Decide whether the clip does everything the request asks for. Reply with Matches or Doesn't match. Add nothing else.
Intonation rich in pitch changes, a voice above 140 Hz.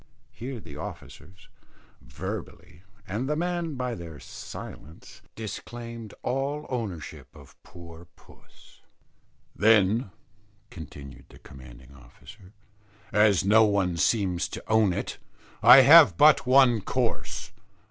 Doesn't match